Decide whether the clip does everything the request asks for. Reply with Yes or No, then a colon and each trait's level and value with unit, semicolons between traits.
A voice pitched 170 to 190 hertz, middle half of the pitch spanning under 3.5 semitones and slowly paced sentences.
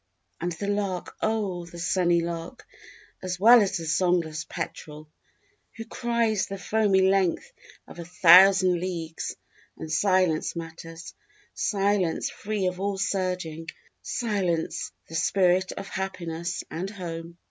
Yes: medium, 185 Hz; average, 2.8 semitones; slow, 130 wpm